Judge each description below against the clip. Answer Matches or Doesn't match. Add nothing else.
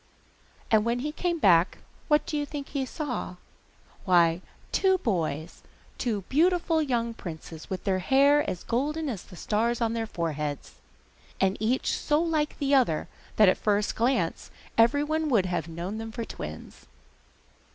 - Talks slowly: Doesn't match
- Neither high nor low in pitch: Doesn't match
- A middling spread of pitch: Doesn't match